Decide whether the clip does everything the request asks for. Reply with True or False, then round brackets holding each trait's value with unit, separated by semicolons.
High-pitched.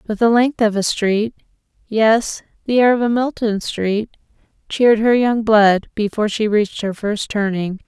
True (220 Hz)